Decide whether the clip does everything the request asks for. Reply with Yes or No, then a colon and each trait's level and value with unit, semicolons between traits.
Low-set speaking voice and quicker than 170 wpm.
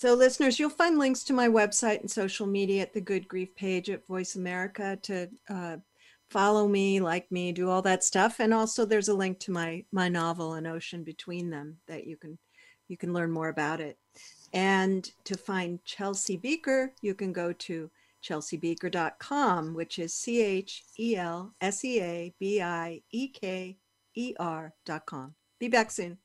No: high, 190 Hz; average, 185 wpm